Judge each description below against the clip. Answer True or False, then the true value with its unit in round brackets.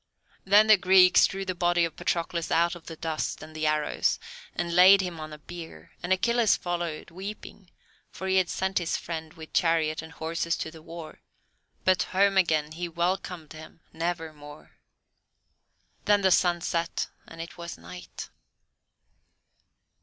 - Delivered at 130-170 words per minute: True (160 wpm)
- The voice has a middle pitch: True (170 Hz)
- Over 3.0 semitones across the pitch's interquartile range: False (2.5 semitones)